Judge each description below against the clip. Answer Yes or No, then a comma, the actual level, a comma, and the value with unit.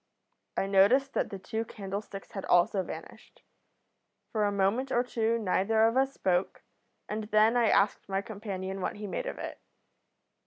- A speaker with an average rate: Yes, average, 165 wpm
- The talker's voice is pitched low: No, high, 210 Hz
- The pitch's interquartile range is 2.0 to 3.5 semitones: Yes, average, 2.8 semitones